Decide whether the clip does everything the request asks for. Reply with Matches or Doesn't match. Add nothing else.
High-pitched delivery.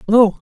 Matches